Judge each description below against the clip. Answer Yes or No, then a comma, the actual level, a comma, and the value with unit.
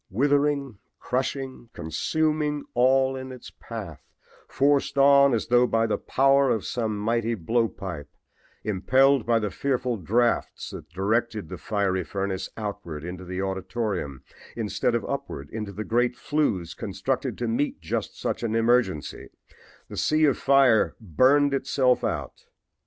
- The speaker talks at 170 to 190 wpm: No, average, 140 wpm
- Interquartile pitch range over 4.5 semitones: Yes, average, 5.2 semitones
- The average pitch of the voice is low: Yes, low, 120 Hz